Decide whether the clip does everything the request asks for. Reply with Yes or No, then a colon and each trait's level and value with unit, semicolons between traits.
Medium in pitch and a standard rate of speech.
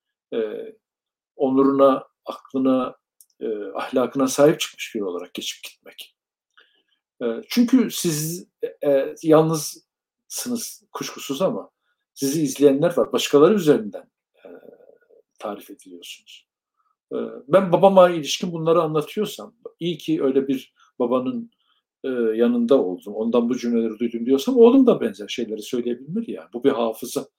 Yes: medium, 160 Hz; average, 125 wpm